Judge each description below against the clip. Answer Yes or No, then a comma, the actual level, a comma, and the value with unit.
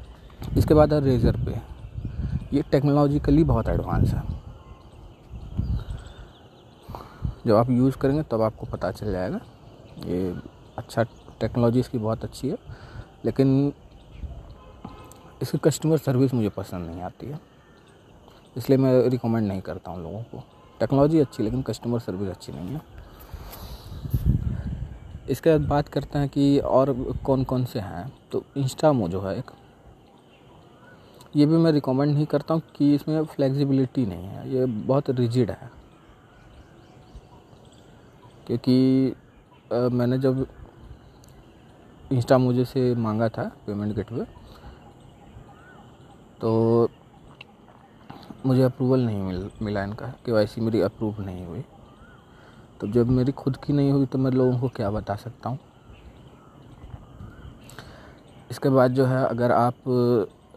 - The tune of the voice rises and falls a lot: No, average, 3.8 semitones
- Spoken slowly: No, average, 130 wpm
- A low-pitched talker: Yes, low, 125 Hz